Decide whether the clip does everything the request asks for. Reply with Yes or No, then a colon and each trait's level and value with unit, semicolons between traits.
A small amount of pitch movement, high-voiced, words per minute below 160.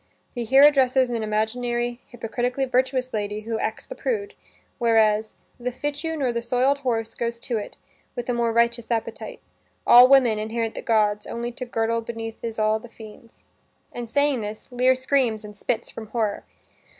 No: narrow, 2.3 semitones; high, 235 Hz; average, 175 wpm